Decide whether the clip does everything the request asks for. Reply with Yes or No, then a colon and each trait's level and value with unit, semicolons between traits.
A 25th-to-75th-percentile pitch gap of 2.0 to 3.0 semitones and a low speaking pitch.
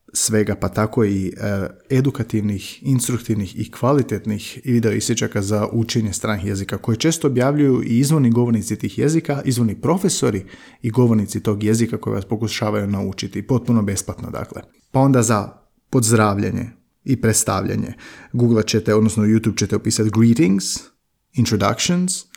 Yes: narrow, 2.6 semitones; low, 110 Hz